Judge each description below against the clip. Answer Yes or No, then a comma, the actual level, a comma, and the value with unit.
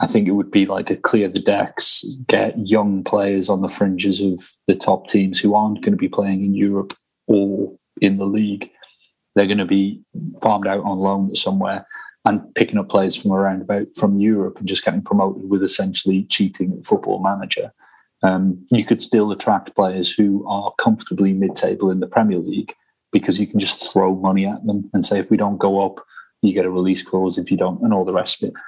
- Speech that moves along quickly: Yes, fast, 215 wpm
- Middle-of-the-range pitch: No, low, 100 Hz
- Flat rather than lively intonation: Yes, narrow, 1.1 semitones